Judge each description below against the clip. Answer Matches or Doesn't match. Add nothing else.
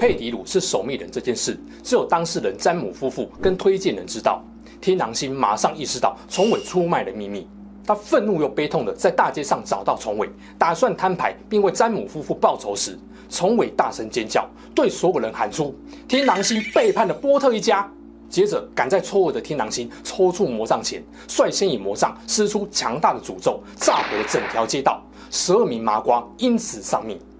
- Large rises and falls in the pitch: Matches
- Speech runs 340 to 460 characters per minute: Doesn't match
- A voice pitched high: Matches